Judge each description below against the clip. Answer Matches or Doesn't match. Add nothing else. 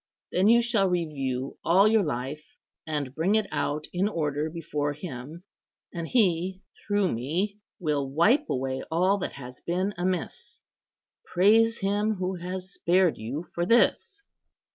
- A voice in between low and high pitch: Matches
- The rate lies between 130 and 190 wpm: Matches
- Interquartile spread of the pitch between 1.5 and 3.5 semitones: Doesn't match